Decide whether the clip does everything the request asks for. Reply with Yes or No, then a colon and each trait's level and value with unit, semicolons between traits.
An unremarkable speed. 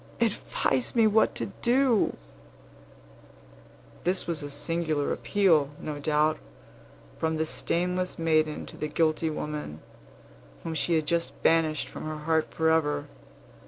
No: slow, 125 wpm